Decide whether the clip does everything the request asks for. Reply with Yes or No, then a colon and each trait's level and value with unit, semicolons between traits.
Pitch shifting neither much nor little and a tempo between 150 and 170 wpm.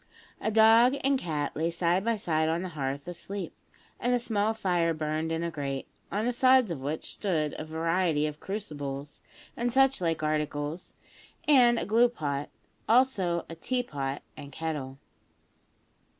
No: wide, 6.5 semitones; average, 165 wpm